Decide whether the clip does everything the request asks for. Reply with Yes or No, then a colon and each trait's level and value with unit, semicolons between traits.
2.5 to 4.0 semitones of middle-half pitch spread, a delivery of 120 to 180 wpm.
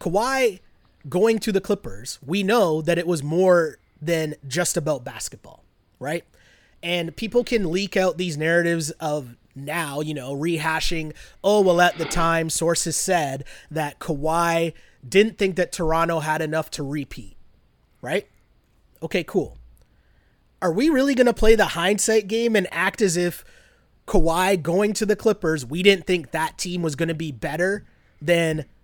Yes: average, 3.7 semitones; average, 160 wpm